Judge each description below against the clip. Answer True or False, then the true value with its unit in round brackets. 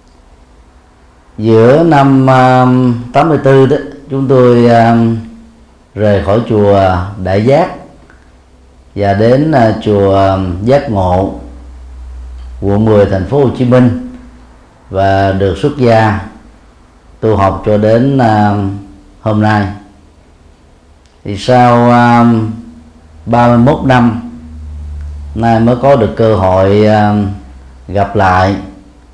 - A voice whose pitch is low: True (100 Hz)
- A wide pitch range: True (6.4 semitones)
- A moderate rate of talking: False (105 wpm)